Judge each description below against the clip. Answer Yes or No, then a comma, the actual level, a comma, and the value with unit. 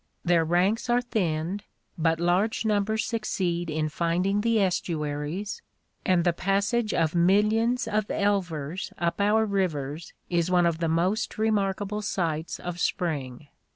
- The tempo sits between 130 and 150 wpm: Yes, slow, 135 wpm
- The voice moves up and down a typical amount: Yes, average, 4.0 semitones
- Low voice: No, medium, 180 Hz